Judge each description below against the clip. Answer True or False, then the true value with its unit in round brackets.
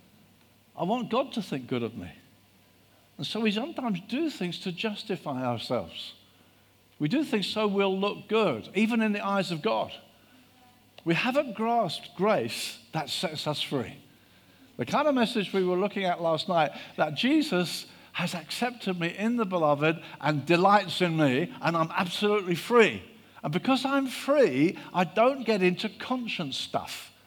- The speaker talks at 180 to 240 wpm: False (165 wpm)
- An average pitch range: False (7.0 semitones)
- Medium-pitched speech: True (180 Hz)